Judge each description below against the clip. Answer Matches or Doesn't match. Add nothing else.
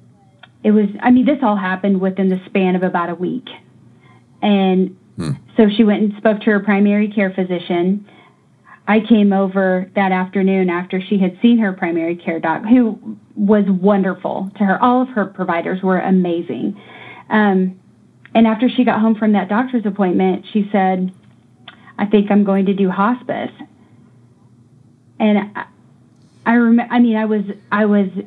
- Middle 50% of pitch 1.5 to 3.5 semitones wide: Matches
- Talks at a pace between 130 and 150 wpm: Doesn't match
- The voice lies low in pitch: Doesn't match